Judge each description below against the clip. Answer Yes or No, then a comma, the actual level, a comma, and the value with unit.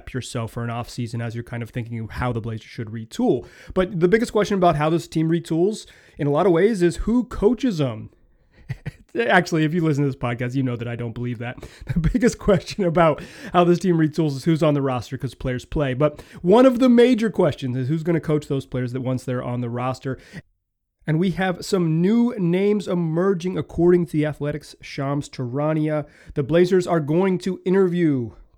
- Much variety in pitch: Yes, wide, 6.2 semitones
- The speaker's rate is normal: No, fast, 210 wpm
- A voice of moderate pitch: Yes, medium, 155 Hz